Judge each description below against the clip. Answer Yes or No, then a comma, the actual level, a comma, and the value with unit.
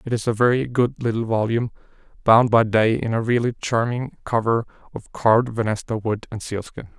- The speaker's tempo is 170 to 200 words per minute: Yes, average, 180 wpm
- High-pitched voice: No, low, 115 Hz